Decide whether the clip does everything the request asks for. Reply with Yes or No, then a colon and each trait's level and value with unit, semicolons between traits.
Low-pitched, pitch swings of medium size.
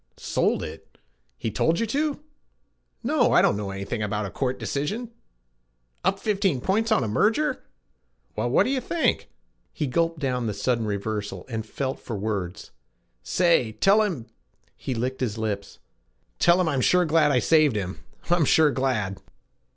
No: low, 130 Hz; wide, 8.5 semitones